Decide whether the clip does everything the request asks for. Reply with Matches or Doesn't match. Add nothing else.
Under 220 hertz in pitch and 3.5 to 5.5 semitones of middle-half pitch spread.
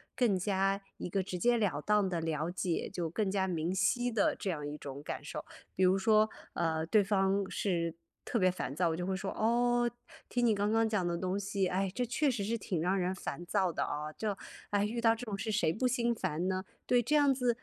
Matches